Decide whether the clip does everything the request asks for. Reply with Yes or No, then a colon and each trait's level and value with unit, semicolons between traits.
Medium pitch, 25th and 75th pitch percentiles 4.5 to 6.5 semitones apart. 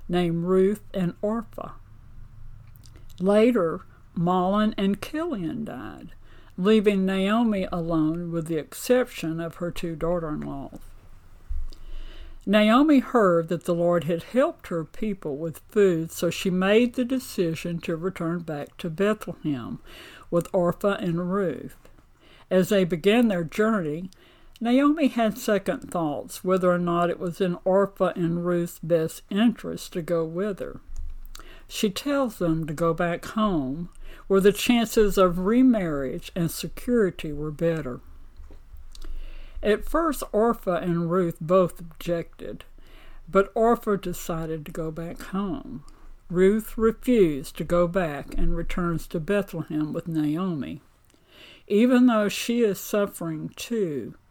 No: medium, 180 Hz; average, 4.1 semitones